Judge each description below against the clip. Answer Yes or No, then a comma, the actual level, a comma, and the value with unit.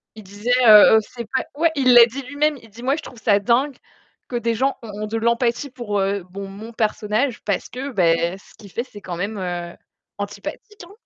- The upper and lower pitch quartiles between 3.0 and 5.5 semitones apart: Yes, average, 3.9 semitones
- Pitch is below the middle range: No, high, 225 Hz